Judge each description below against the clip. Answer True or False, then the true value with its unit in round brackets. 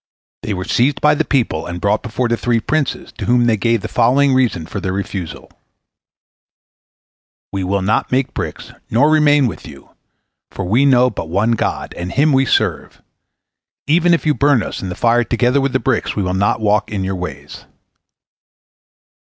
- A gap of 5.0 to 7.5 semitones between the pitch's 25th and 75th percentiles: True (5.5 semitones)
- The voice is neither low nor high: False (115 Hz)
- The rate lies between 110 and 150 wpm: False (185 wpm)